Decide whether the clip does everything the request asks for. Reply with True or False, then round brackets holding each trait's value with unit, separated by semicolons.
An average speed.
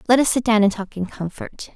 False (275 wpm)